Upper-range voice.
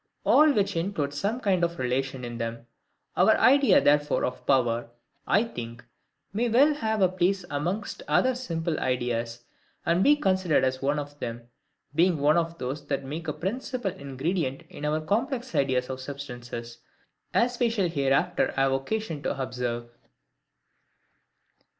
No: medium, 150 Hz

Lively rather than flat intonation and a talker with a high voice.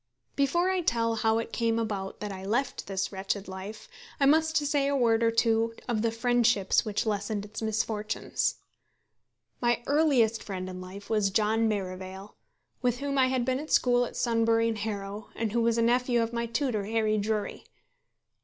No: average, 2.8 semitones; high, 225 Hz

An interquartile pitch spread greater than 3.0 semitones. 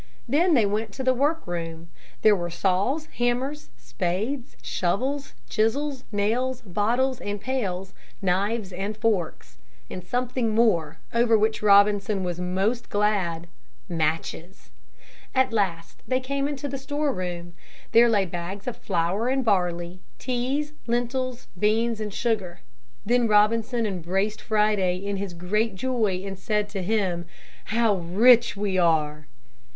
Yes: average, 5.0 semitones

